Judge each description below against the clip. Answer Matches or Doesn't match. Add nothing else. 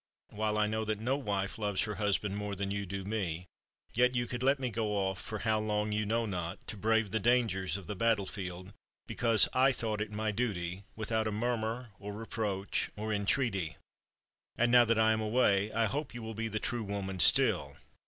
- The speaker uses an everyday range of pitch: Doesn't match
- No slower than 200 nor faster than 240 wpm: Matches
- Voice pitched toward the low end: Matches